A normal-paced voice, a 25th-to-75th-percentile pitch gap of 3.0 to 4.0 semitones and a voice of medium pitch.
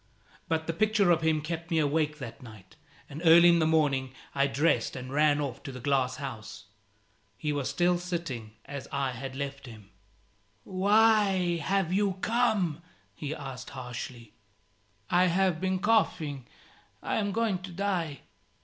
No: average, 160 wpm; average, 5.1 semitones; medium, 155 Hz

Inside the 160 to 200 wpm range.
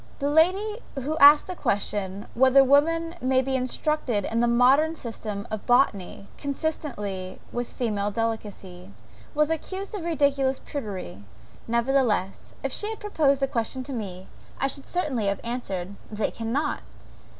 No: average, 145 wpm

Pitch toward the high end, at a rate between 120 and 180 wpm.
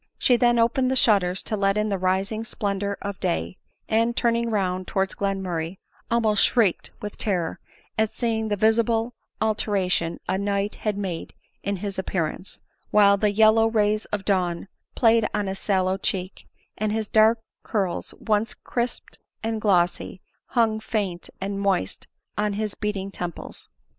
Yes: high, 205 Hz; average, 160 wpm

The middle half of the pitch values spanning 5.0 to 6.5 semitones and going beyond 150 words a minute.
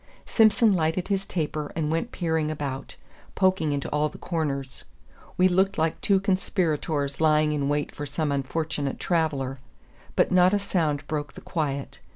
No: average, 3.8 semitones; average, 160 wpm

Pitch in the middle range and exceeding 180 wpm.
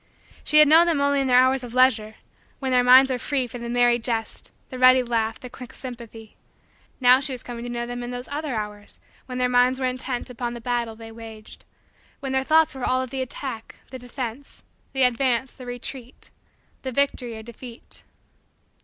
No: very high, 250 Hz; fast, 205 wpm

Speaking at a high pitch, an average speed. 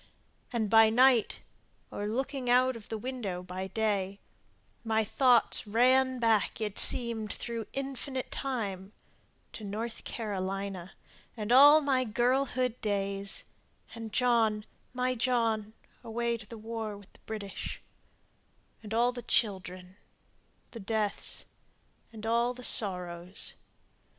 No: high, 225 Hz; slow, 120 wpm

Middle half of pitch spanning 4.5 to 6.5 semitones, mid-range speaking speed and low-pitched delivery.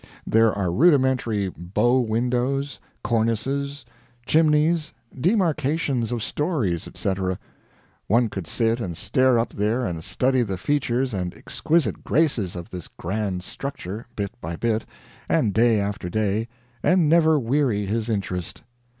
No: wide, 5.6 semitones; slow, 130 wpm; low, 115 Hz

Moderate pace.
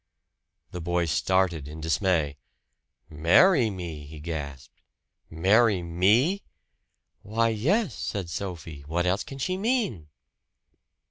No: slow, 110 wpm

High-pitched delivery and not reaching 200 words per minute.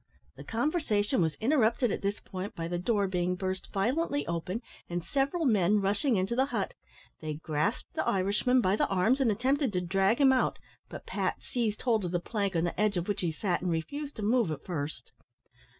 No: high, 200 Hz; fast, 205 wpm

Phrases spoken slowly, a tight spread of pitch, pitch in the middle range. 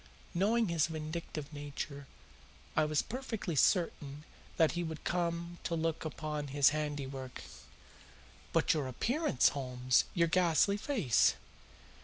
No: slow, 120 wpm; average, 3.2 semitones; medium, 155 Hz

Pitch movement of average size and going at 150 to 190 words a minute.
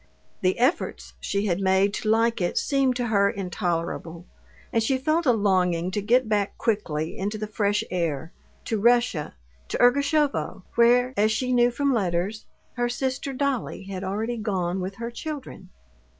Yes: average, 4.5 semitones; average, 165 wpm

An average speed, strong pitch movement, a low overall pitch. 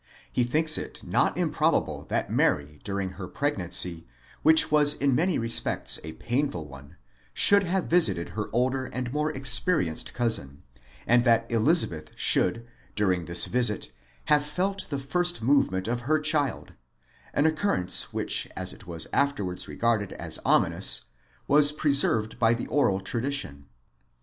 Yes: average, 145 wpm; wide, 7.9 semitones; low, 120 Hz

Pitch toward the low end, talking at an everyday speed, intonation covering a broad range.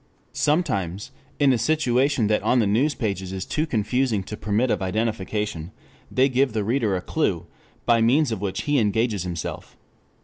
No: low, 110 Hz; average, 170 wpm; average, 4.7 semitones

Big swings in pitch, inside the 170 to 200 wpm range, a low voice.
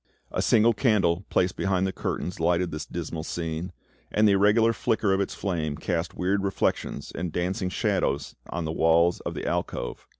No: average, 3.0 semitones; average, 175 wpm; very low, 90 Hz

